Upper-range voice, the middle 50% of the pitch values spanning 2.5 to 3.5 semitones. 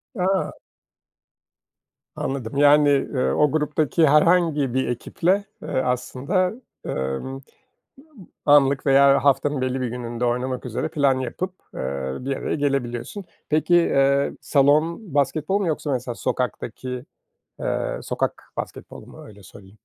No: medium, 140 Hz; average, 3.1 semitones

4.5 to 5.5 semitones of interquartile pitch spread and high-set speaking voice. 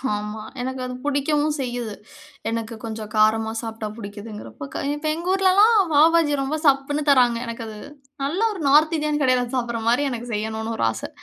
Yes: average, 5.1 semitones; high, 245 Hz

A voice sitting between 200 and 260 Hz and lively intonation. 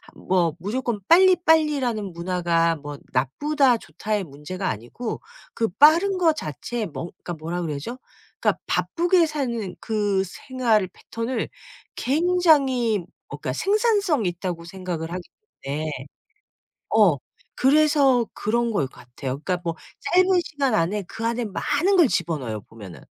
Yes: high, 215 Hz; wide, 9.0 semitones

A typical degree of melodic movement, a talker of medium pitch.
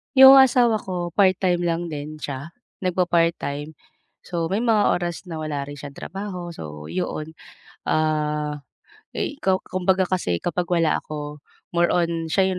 Yes: average, 3.4 semitones; medium, 170 Hz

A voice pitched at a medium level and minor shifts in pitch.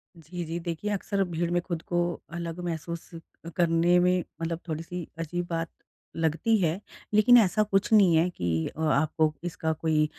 Yes: medium, 170 Hz; narrow, 1.9 semitones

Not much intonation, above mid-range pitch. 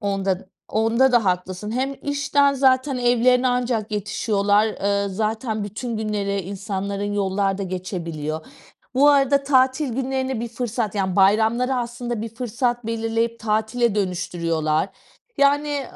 No: average, 4.1 semitones; high, 220 Hz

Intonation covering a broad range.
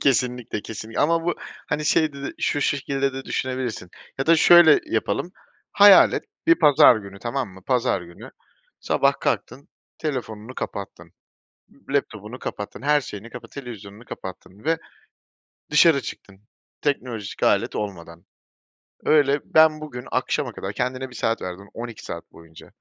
Yes: wide, 5.7 semitones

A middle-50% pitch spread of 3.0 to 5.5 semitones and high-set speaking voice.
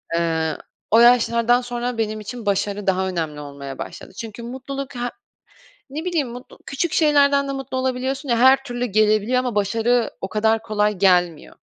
Yes: average, 4.1 semitones; high, 235 Hz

